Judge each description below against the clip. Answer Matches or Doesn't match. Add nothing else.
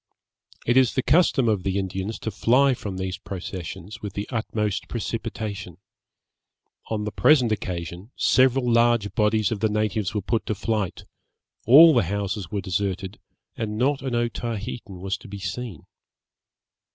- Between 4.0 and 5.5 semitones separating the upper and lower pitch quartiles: Doesn't match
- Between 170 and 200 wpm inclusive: Doesn't match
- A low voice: Matches